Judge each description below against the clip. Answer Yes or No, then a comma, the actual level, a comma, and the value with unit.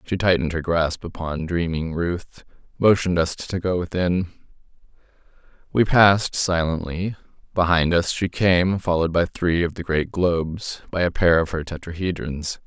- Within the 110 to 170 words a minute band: Yes, average, 150 wpm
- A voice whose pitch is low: Yes, very low, 85 Hz